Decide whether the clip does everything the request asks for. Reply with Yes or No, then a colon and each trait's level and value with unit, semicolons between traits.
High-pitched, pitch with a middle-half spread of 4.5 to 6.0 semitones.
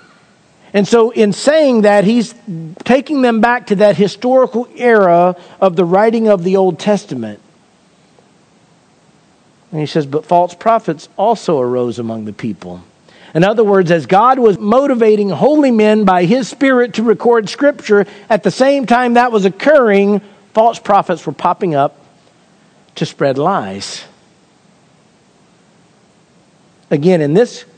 Yes: high, 200 Hz; average, 4.9 semitones